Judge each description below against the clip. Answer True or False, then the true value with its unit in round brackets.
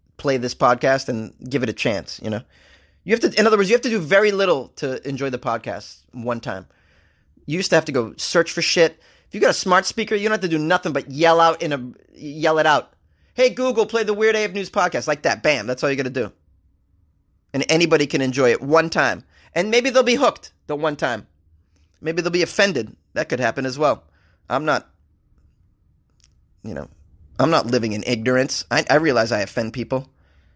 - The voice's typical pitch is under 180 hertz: True (140 Hz)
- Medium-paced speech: False (220 wpm)